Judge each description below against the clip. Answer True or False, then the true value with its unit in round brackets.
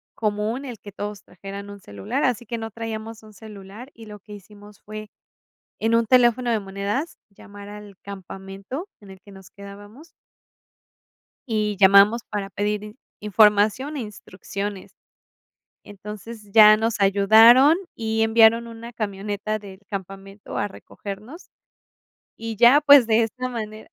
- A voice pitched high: True (210 Hz)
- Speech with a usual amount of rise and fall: False (2.2 semitones)